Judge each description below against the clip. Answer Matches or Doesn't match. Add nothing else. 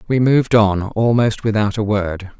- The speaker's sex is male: Matches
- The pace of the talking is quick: Doesn't match